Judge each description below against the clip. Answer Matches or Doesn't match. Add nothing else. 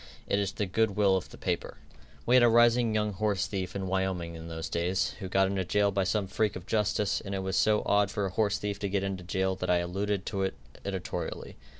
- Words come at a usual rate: Doesn't match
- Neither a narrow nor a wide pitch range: Doesn't match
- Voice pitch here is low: Matches